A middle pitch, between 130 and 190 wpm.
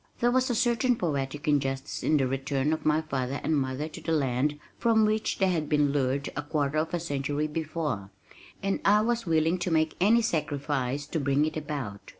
No: medium, 150 Hz; average, 200 wpm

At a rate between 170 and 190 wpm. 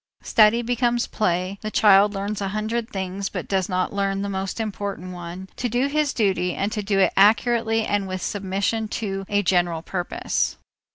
Yes: average, 180 wpm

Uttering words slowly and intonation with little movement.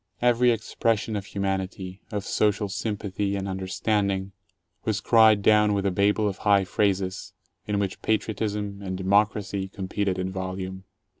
No: average, 145 wpm; narrow, 1.8 semitones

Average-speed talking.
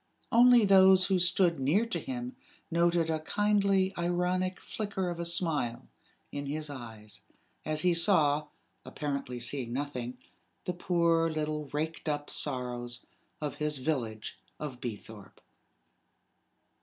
No: slow, 125 wpm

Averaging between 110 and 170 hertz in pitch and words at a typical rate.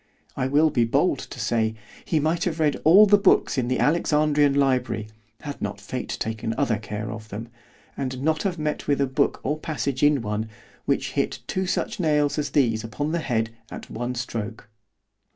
Yes: low, 135 Hz; average, 190 wpm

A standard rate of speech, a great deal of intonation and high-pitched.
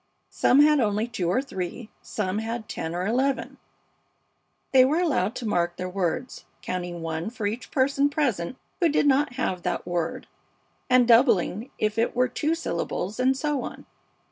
Yes: average, 170 wpm; wide, 6.5 semitones; high, 230 Hz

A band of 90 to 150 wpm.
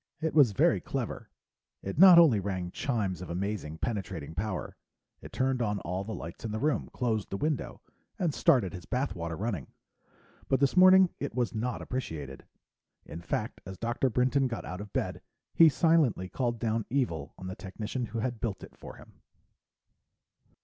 No: average, 175 wpm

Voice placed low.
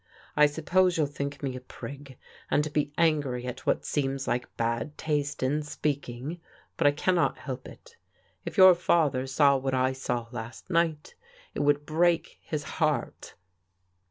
No: medium, 145 Hz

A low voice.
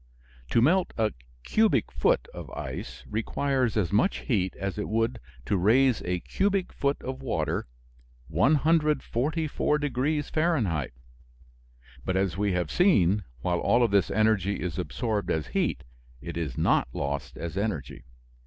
Yes: low, 110 Hz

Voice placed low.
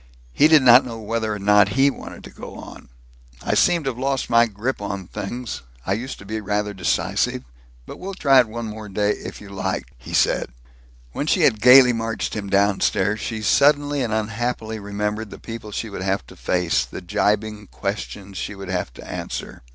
Yes: low, 110 Hz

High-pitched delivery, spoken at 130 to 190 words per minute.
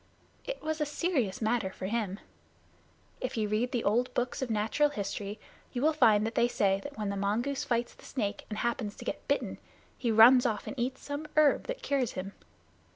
No: high, 235 Hz; average, 200 wpm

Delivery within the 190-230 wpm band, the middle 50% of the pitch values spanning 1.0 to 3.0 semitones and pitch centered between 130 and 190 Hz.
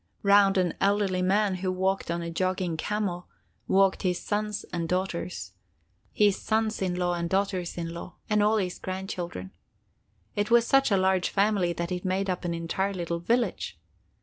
No: average, 175 wpm; narrow, 2.4 semitones; medium, 185 Hz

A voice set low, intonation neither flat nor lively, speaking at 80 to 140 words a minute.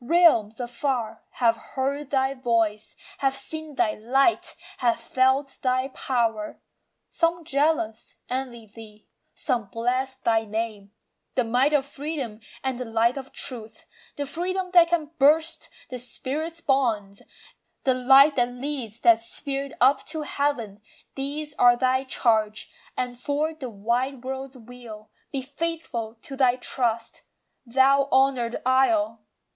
No: very high, 255 Hz; average, 3.3 semitones; slow, 135 wpm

